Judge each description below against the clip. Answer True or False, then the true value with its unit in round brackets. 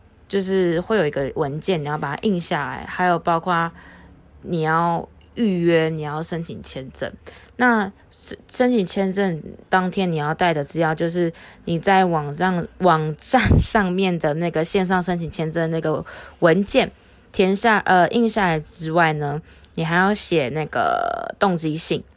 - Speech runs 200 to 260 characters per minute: True (225 characters per minute)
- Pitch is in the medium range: True (175 Hz)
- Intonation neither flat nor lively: True (3.5 semitones)